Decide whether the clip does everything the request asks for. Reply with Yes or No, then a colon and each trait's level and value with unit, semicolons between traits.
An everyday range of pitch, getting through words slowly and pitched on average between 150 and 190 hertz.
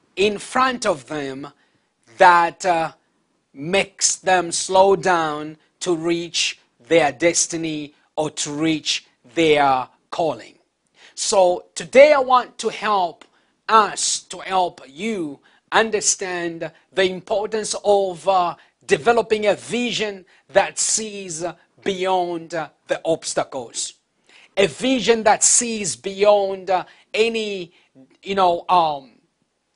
Yes: average, 4.1 semitones; slow, 105 wpm; medium, 185 Hz